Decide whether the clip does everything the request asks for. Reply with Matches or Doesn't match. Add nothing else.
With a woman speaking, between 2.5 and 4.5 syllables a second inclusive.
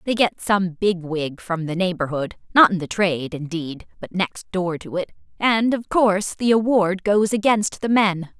Matches